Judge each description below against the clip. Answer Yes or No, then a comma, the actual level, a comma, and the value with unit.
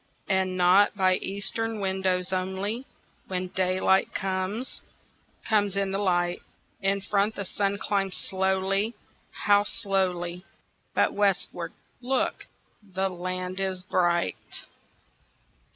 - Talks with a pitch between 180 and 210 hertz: Yes, high, 190 Hz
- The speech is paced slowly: Yes, slow, 95 wpm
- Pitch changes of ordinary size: No, narrow, 1.6 semitones